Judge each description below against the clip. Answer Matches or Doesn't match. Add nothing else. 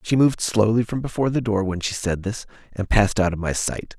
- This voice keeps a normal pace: Doesn't match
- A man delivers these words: Matches